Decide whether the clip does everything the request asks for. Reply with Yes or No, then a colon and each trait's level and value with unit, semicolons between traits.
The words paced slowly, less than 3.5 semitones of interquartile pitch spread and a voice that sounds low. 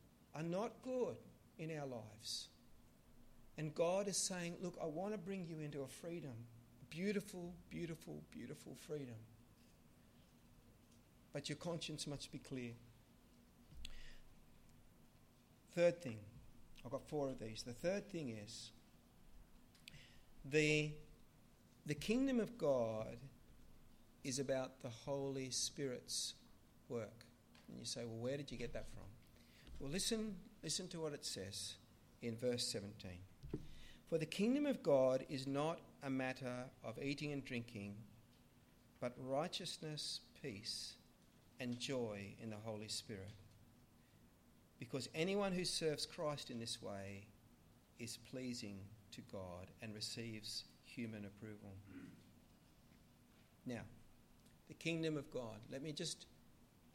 No: slow, 125 wpm; wide, 5.5 semitones; low, 125 Hz